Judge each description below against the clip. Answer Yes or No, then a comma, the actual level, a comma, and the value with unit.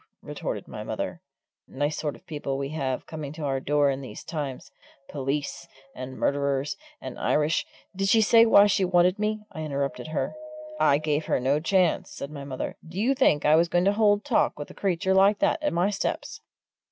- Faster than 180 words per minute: Yes, average, 200 wpm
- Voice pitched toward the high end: No, medium, 155 Hz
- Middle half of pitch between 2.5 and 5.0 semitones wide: No, wide, 5.5 semitones